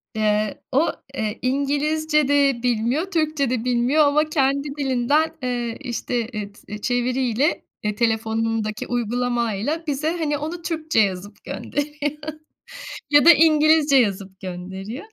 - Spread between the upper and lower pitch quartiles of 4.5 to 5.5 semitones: Yes, average, 5.1 semitones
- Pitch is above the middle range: Yes, very high, 255 Hz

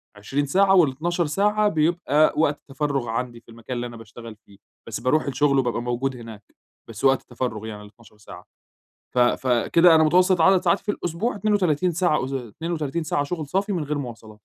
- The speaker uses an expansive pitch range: Yes, wide, 6.3 semitones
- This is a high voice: No, medium, 140 Hz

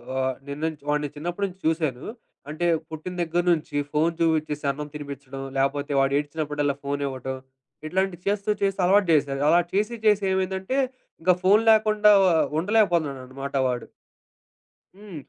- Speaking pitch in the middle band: Yes, medium, 155 Hz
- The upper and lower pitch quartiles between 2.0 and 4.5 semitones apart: No, average, 5.0 semitones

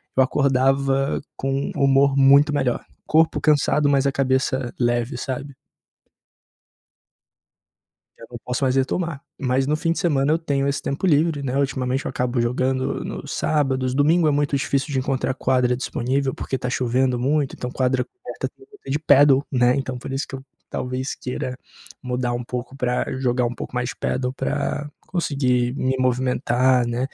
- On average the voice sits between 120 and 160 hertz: Yes, low, 135 Hz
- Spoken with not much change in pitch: Yes, narrow, 1.9 semitones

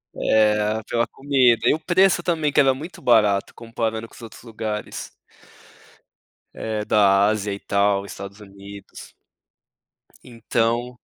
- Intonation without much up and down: No, average, 3.3 semitones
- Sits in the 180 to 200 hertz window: No, low, 110 Hz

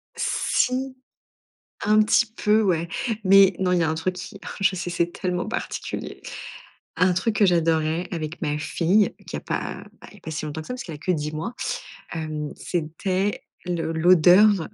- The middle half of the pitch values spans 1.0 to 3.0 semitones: No, average, 3.6 semitones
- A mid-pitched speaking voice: Yes, medium, 180 Hz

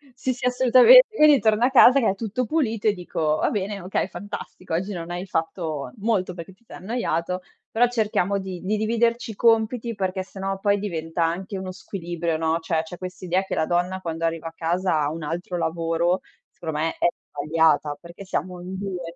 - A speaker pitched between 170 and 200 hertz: Yes, medium, 185 Hz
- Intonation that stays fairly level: No, average, 4.2 semitones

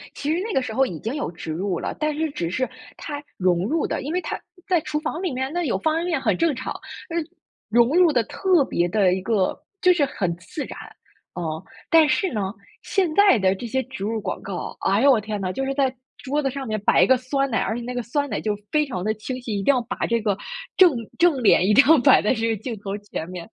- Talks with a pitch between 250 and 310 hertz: Yes, very high, 255 Hz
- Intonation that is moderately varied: No, wide, 6.4 semitones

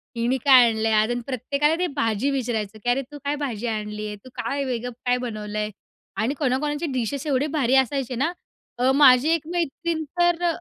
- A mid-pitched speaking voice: No, very high, 255 Hz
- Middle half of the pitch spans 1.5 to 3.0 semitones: No, average, 4.0 semitones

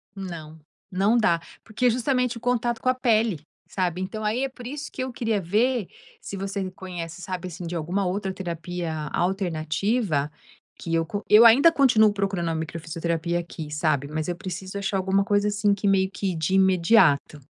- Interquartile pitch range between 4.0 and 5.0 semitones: Yes, average, 4.4 semitones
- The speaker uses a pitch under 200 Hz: Yes, high, 190 Hz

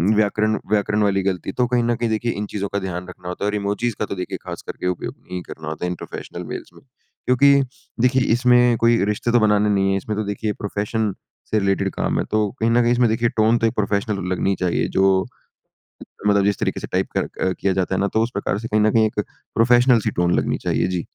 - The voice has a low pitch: Yes, low, 105 Hz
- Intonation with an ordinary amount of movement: Yes, average, 3.0 semitones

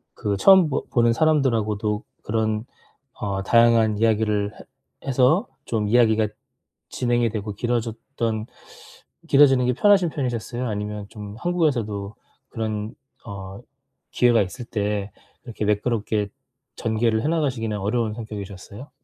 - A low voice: Yes, low, 110 Hz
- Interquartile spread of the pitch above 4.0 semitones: No, average, 2.7 semitones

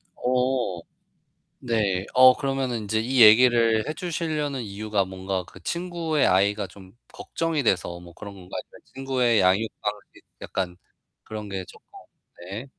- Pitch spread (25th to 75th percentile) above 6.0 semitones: No, average, 5.3 semitones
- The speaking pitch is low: Yes, low, 110 Hz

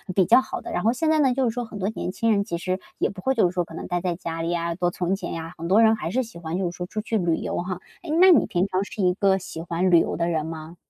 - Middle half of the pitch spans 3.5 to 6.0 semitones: Yes, average, 4.3 semitones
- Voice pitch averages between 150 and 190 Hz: Yes, medium, 185 Hz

